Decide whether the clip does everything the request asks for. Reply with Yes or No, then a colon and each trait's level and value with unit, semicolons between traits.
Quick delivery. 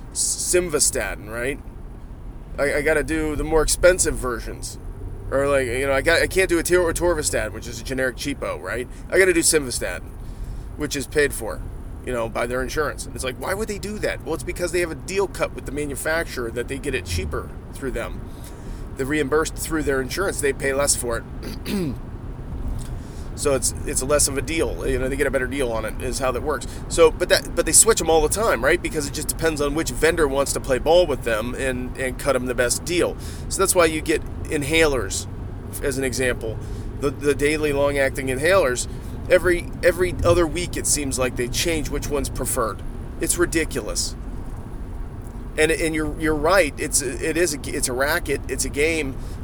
Yes: fast, 210 wpm